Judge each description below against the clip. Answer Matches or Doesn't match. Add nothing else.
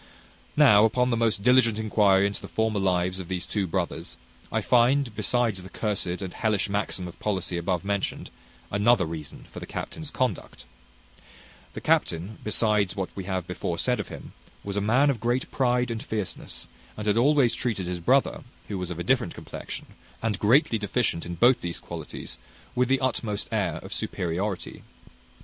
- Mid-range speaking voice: Doesn't match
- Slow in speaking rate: Doesn't match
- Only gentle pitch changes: Doesn't match